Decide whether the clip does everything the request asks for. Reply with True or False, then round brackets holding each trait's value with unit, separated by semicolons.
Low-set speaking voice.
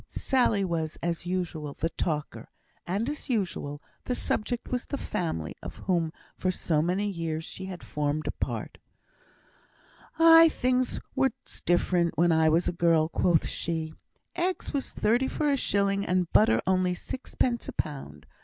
False (180 Hz)